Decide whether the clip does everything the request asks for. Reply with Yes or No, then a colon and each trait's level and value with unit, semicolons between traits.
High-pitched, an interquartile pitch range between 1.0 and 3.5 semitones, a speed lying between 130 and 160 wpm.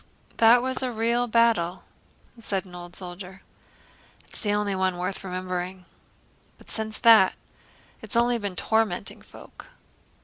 No: high, 205 Hz; average, 4.0 semitones; slow, 135 wpm